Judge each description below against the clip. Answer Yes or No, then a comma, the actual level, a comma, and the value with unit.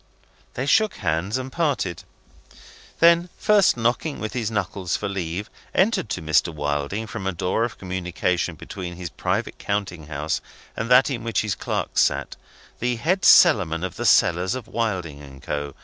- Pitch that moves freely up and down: Yes, wide, 6.1 semitones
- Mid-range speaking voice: No, low, 100 Hz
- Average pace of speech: Yes, average, 165 wpm